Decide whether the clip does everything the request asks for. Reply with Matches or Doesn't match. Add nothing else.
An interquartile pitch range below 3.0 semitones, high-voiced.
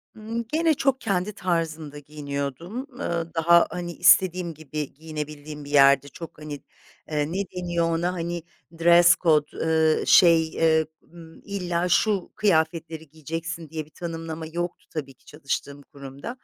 Doesn't match